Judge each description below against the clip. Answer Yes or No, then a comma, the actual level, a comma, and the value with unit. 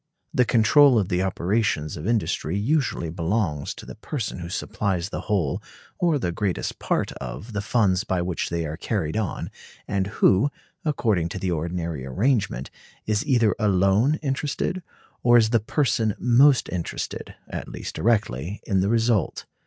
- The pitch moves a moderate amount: Yes, average, 5.0 semitones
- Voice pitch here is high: No, low, 105 Hz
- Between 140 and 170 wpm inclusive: Yes, average, 160 wpm